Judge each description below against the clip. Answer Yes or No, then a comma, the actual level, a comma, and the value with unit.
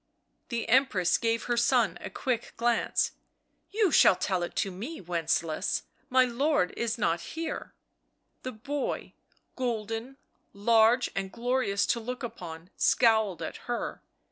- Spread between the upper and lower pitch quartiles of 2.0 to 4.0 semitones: No, average, 4.5 semitones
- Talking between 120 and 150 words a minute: Yes, average, 140 wpm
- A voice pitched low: No, high, 230 Hz